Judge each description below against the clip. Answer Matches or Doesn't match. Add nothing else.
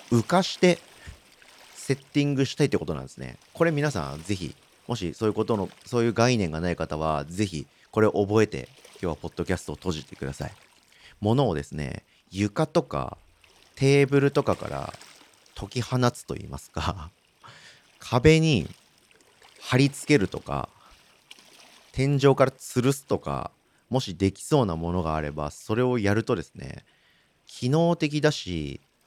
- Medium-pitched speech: Doesn't match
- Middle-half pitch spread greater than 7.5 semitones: Matches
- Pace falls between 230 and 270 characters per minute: Doesn't match